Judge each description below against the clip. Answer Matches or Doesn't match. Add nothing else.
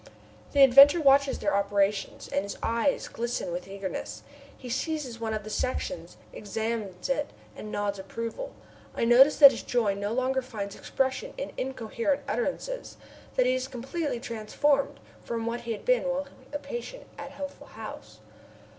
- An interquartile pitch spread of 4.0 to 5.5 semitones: Matches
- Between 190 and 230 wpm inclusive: Doesn't match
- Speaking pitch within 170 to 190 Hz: Doesn't match